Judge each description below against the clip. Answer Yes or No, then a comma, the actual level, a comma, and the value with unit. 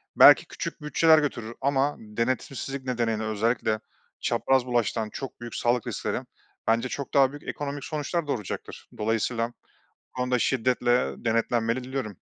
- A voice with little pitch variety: No, average, 3.1 semitones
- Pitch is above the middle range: No, low, 125 Hz